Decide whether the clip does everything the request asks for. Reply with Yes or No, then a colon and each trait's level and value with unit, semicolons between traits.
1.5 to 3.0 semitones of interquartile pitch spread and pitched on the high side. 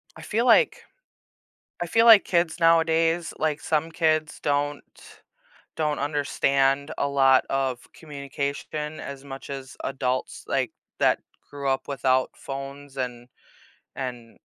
No: average, 2.7 semitones; medium, 140 Hz